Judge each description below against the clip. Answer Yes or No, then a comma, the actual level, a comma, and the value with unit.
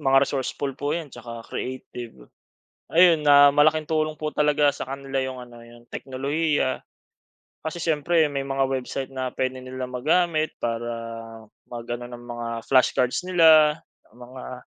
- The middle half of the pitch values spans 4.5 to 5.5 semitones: No, average, 3.3 semitones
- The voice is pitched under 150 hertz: Yes, low, 135 Hz